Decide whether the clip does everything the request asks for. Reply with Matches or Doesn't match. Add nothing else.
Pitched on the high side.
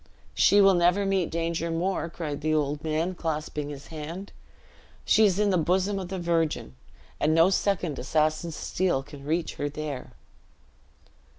Doesn't match